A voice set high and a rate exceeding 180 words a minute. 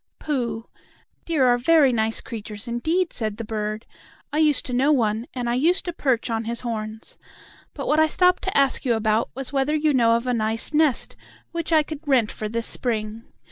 Yes: high, 245 Hz; fast, 205 wpm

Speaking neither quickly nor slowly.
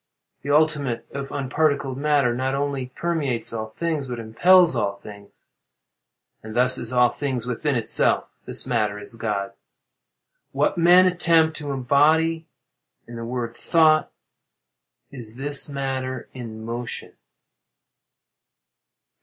No: slow, 120 wpm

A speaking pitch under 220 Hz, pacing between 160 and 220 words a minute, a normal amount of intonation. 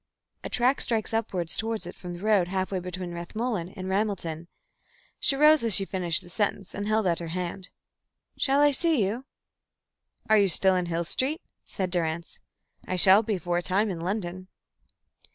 Yes: high, 190 Hz; average, 180 wpm; average, 3.8 semitones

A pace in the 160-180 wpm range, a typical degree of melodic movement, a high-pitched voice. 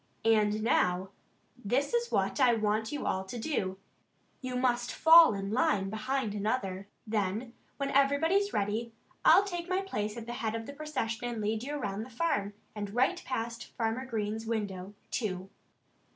Yes: average, 175 wpm; average, 4.3 semitones; high, 225 Hz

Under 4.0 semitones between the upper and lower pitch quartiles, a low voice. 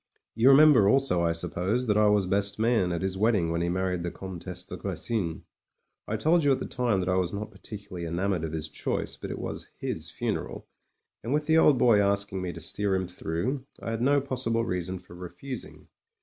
No: average, 4.8 semitones; low, 100 Hz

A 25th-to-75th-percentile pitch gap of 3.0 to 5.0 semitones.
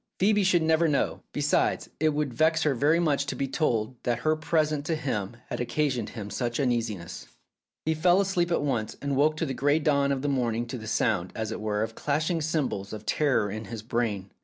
No: wide, 5.5 semitones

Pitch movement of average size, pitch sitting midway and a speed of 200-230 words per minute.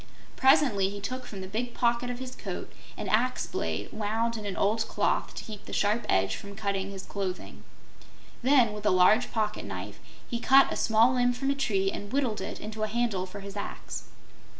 No: average, 3.4 semitones; high, 215 Hz; fast, 205 wpm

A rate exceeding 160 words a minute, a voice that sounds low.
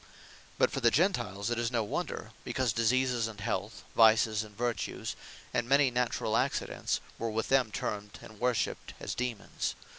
No: average, 155 wpm; low, 115 Hz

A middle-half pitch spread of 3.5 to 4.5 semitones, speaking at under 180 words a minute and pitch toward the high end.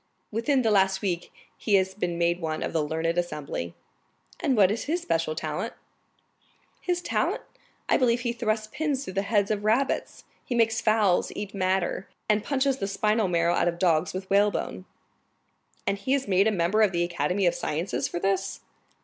No: average, 4.2 semitones; average, 185 wpm; high, 195 Hz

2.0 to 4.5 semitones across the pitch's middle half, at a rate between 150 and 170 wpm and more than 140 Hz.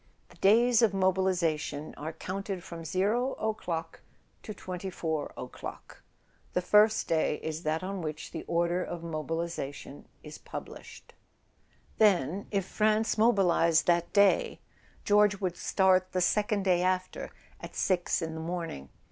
No: average, 3.6 semitones; slow, 135 wpm; medium, 185 Hz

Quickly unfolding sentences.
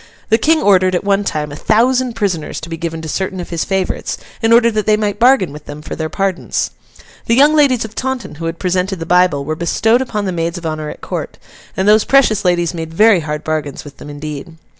Yes: fast, 235 wpm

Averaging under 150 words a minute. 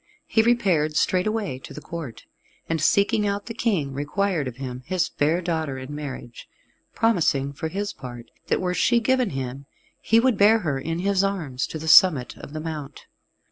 No: average, 180 wpm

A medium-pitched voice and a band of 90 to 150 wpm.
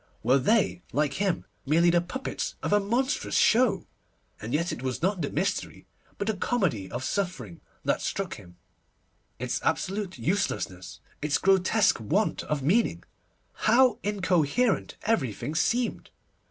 Yes: medium, 180 Hz; average, 140 wpm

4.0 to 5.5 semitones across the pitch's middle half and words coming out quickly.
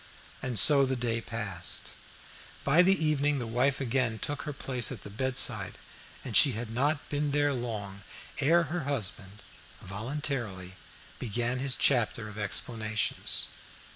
No: average, 4.6 semitones; average, 145 wpm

